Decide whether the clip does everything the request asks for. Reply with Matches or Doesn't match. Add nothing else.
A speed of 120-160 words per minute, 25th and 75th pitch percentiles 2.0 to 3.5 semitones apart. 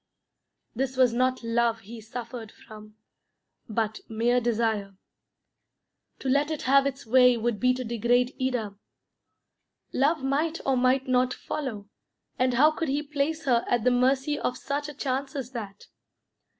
Matches